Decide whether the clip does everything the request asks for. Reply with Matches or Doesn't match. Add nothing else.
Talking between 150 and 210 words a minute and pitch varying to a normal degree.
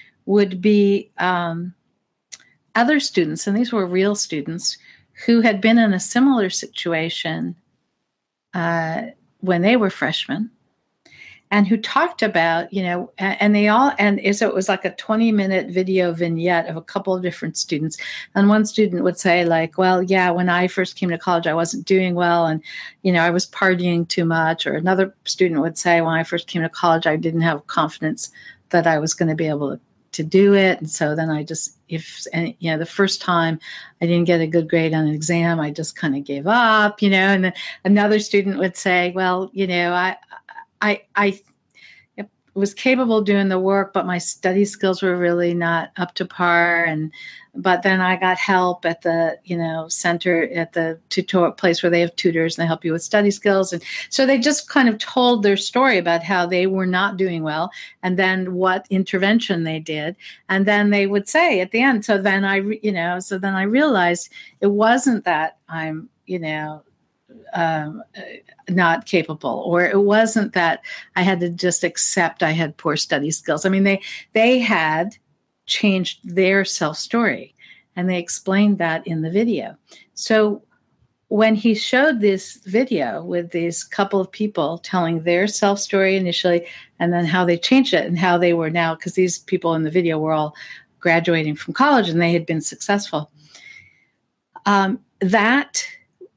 Matches